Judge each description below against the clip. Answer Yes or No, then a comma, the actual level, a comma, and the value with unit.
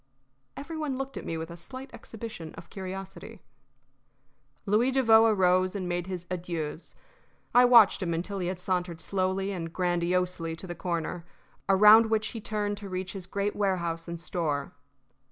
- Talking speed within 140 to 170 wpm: Yes, average, 165 wpm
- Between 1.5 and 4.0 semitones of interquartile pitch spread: Yes, average, 3.4 semitones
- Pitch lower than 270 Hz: Yes, medium, 185 Hz